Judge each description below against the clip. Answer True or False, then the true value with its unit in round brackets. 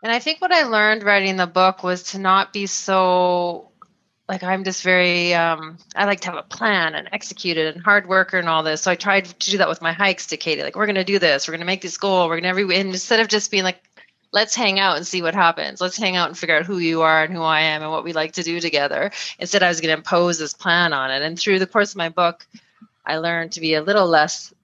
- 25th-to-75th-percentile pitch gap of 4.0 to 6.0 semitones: False (3.1 semitones)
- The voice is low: False (180 Hz)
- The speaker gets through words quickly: True (285 wpm)